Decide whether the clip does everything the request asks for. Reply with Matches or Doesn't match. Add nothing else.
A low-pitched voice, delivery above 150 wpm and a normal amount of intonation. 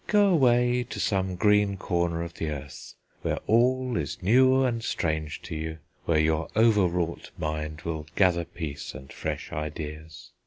Doesn't match